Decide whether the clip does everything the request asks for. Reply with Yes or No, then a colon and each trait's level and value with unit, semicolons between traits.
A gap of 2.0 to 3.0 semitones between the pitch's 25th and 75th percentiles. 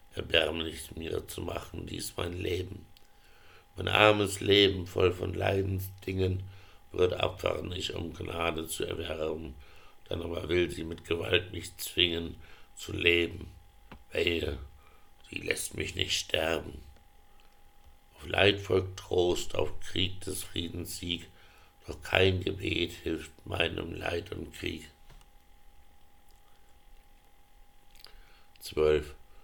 Yes: average, 2.7 semitones